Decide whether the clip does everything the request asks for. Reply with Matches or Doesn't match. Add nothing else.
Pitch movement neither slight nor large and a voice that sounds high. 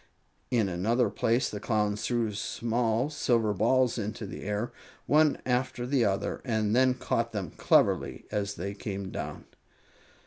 Doesn't match